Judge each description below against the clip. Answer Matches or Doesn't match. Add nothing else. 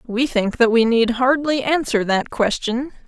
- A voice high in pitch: Matches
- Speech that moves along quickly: Doesn't match